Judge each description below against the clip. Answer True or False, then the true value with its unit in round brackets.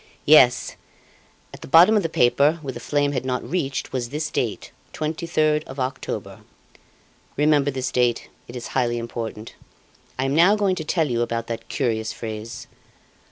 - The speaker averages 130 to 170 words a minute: True (165 wpm)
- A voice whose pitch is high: False (130 Hz)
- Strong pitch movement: False (4.3 semitones)